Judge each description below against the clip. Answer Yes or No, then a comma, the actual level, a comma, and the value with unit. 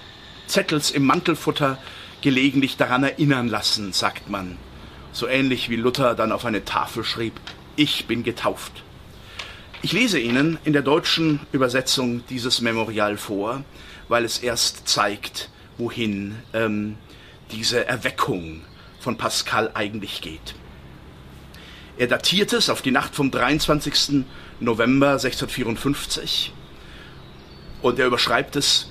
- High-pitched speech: No, low, 115 Hz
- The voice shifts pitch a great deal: Yes, wide, 5.7 semitones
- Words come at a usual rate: No, slow, 120 wpm